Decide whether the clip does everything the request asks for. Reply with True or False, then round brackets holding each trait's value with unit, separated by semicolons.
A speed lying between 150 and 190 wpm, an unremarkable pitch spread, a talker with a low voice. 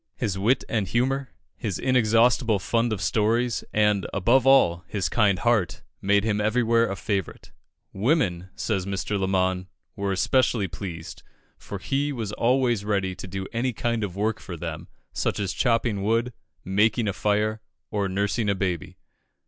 True (155 wpm; 3.3 semitones; 105 Hz)